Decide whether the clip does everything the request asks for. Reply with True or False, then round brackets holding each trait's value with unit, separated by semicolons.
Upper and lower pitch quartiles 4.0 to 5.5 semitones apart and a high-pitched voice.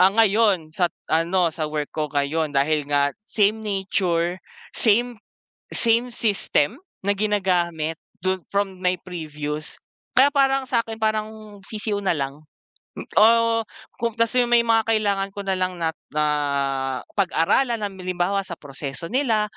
True (5.1 semitones; 195 Hz)